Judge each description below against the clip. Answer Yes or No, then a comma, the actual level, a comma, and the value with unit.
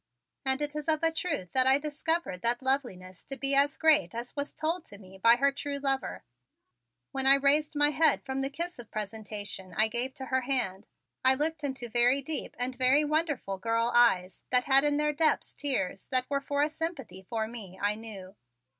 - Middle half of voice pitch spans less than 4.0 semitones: No, average, 4.4 semitones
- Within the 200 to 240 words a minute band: Yes, fast, 205 wpm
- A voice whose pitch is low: No, very high, 265 Hz